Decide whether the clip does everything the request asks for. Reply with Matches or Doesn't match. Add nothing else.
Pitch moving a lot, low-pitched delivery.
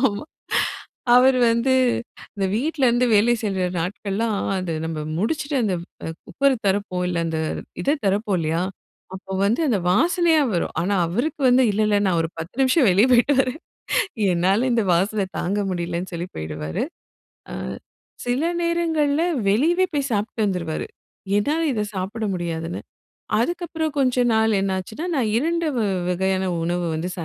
Doesn't match